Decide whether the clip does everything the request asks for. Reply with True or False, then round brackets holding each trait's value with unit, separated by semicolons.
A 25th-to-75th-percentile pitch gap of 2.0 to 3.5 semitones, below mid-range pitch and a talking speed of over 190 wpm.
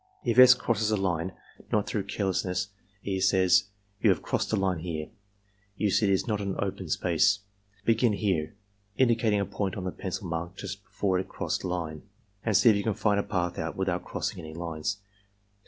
True (2.7 semitones; 95 Hz; 200 wpm)